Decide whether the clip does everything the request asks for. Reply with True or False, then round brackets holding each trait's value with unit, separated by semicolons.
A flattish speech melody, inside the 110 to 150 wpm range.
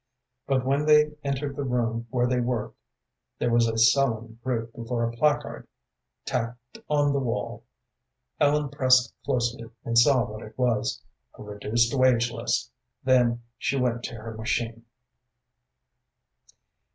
True (2.2 semitones; 140 wpm)